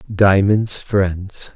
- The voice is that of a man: Yes, male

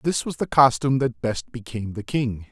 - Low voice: Yes, low, 120 Hz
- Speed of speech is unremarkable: No, fast, 215 wpm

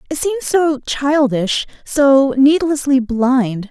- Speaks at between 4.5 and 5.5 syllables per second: No, 3.1 syllables/s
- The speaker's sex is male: No, female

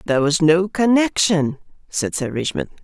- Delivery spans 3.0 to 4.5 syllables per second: No, 4.8 syllables/s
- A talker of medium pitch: Yes, medium, 160 Hz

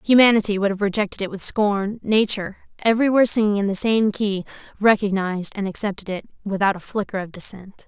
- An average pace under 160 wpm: No, average, 175 wpm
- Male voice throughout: No, female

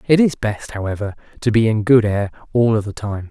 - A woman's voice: No, male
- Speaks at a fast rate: Yes, fast, 235 wpm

